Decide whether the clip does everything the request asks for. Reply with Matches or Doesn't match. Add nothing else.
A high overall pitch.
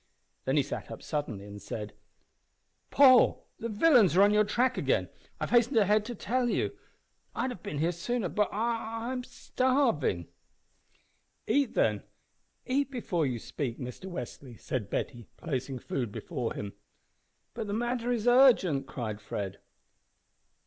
Matches